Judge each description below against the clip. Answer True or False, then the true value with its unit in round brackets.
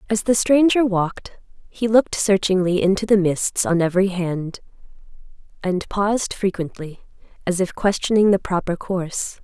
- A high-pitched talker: True (195 Hz)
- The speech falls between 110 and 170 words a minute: True (140 wpm)